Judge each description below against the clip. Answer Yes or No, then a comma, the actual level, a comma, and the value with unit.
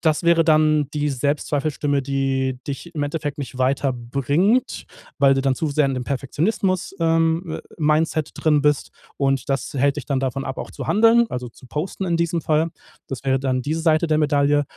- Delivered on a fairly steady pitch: No, average, 3.0 semitones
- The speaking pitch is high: No, medium, 145 Hz